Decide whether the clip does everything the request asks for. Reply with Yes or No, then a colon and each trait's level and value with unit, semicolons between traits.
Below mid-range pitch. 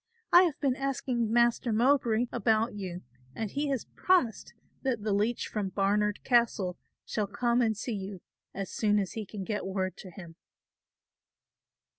No: high, 220 Hz